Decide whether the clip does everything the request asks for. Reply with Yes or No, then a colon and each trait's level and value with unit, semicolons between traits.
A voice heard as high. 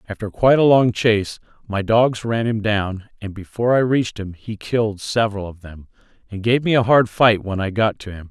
No: low, 110 Hz